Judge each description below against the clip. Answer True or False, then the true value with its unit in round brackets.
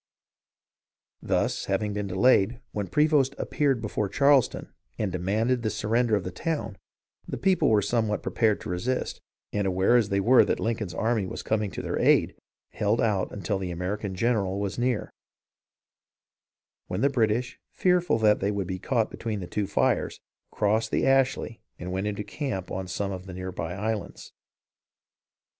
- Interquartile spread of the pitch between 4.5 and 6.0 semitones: False (3.7 semitones)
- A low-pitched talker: True (105 Hz)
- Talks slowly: False (165 wpm)